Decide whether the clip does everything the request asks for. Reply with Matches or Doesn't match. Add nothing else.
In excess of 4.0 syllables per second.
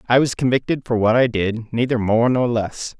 Matches